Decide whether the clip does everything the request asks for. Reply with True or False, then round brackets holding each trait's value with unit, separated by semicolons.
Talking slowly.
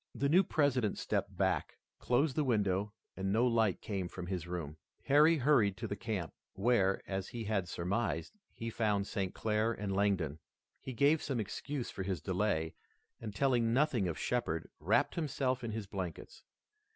False (170 wpm)